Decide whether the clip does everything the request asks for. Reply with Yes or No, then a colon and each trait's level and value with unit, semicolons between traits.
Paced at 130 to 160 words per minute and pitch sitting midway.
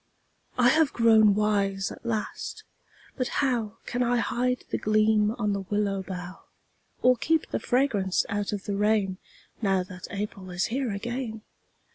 No: average, 155 wpm; high, 215 Hz